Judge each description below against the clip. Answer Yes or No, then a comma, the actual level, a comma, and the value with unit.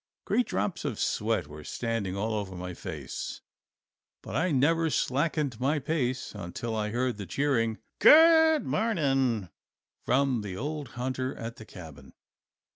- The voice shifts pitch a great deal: Yes, wide, 5.8 semitones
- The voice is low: Yes, low, 125 Hz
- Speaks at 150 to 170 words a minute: No, average, 140 wpm